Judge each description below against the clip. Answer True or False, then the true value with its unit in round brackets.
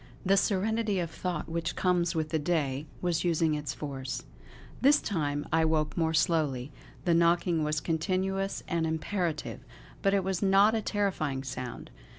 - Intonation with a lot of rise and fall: False (3.8 semitones)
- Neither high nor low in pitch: True (165 Hz)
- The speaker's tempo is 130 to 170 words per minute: True (160 wpm)